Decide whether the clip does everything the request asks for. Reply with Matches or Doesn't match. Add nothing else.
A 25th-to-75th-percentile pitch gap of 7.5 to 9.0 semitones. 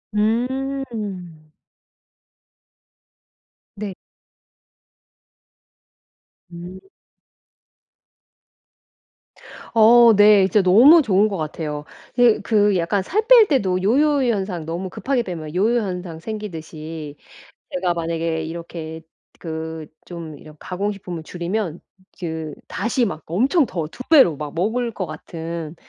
Doesn't match